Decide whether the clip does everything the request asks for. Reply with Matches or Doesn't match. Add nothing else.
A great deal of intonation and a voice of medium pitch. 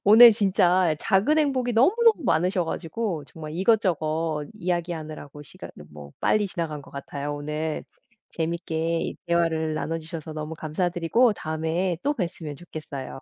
Doesn't match